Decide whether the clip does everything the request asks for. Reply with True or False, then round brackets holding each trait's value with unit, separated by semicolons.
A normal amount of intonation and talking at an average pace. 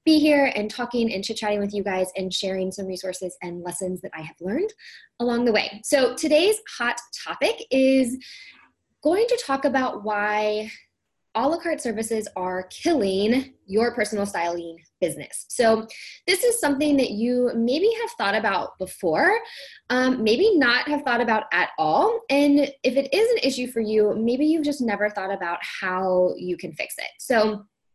False (6.4 semitones; 175 wpm)